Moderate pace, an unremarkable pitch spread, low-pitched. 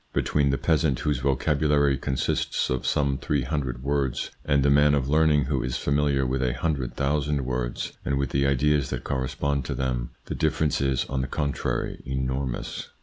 No: average, 185 wpm; narrow, 1.9 semitones; very low, 70 Hz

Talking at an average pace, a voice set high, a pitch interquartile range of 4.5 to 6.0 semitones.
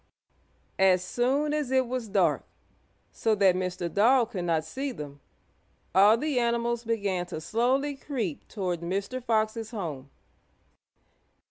No: slow, 130 wpm; high, 220 Hz; average, 5.3 semitones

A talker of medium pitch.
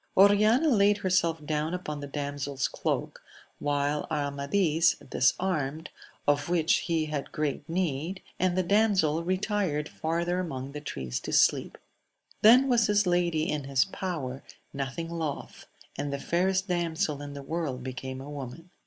Yes: medium, 160 Hz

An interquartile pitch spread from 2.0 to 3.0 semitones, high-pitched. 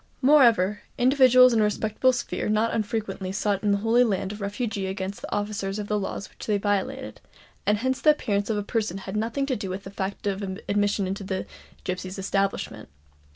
Yes: narrow, 2.6 semitones; high, 205 Hz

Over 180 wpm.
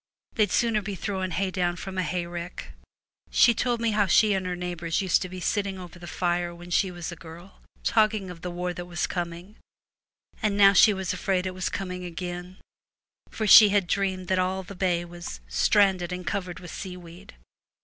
Yes: average, 200 wpm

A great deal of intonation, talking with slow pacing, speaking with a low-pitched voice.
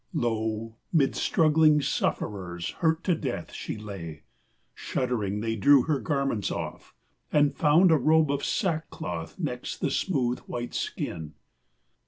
Yes: wide, 6.6 semitones; slow, 130 wpm; low, 125 Hz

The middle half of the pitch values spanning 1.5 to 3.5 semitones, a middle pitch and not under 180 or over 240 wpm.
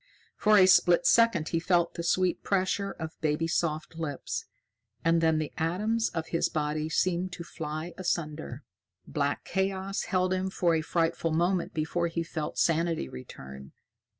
No: average, 2.8 semitones; medium, 170 Hz; average, 155 wpm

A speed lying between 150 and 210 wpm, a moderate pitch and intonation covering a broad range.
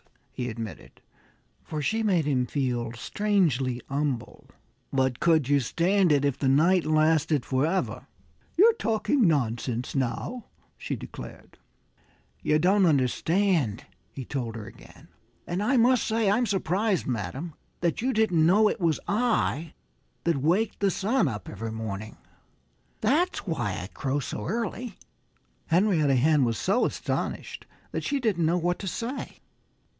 No: average, 140 wpm; medium, 160 Hz; wide, 7.6 semitones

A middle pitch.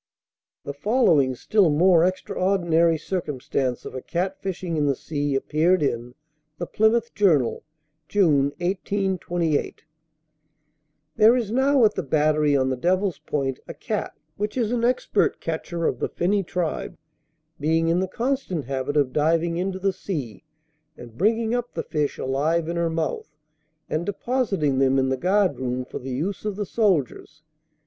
Yes: medium, 170 Hz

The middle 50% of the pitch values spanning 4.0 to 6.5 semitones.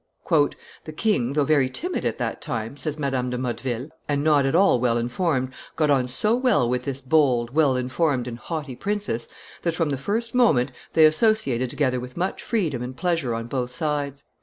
Yes: average, 4.3 semitones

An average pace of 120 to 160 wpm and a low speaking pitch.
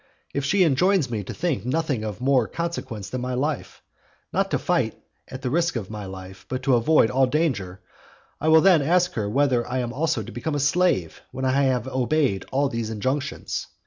No: fast, 205 wpm; low, 130 Hz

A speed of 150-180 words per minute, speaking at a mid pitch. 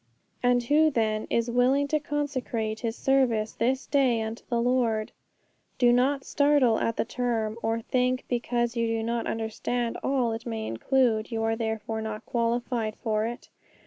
No: average, 165 wpm; high, 235 Hz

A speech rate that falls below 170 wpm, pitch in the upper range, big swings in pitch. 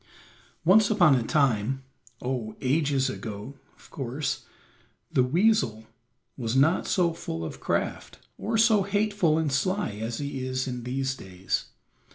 No: average, 140 wpm; low, 135 Hz; wide, 5.9 semitones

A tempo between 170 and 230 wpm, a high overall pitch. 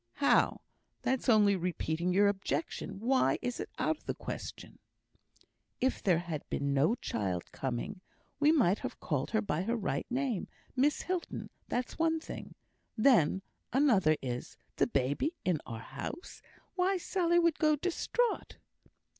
No: average, 145 wpm; high, 215 Hz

